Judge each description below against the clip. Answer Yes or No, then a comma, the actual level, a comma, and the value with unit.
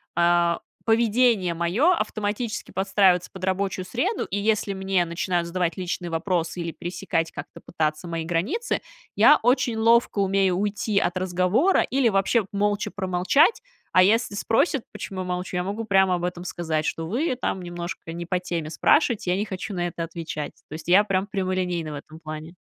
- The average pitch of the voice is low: No, medium, 185 Hz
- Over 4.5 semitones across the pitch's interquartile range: No, average, 3.2 semitones